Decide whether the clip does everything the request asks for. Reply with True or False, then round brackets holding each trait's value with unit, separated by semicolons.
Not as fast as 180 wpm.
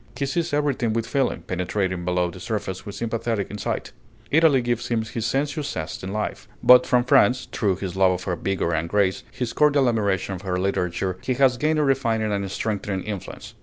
False (200 wpm)